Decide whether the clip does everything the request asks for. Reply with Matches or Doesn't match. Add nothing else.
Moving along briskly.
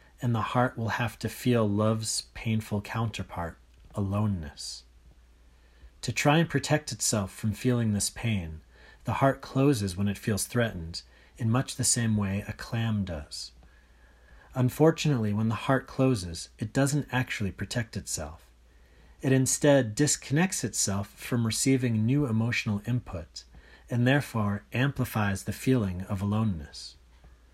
Doesn't match